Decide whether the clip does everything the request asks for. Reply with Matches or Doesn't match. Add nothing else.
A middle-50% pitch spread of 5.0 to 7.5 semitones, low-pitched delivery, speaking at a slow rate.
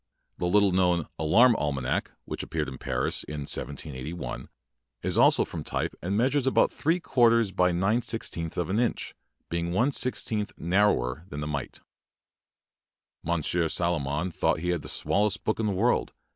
Doesn't match